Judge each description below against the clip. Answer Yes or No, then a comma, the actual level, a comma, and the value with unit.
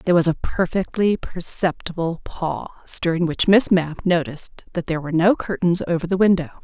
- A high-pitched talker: No, medium, 175 Hz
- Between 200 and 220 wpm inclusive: No, average, 170 wpm